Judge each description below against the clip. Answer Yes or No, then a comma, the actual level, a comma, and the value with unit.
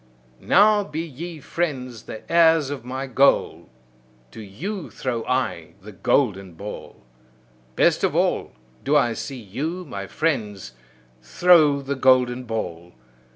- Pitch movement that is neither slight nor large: No, wide, 6.4 semitones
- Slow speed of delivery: Yes, slow, 130 wpm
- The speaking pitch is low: Yes, low, 130 Hz